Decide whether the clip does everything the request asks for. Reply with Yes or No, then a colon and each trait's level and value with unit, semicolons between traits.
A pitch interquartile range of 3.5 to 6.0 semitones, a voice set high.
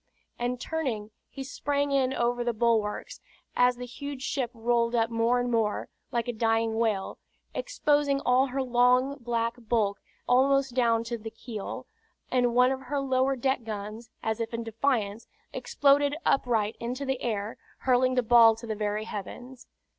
No: narrow, 2.5 semitones; high, 240 Hz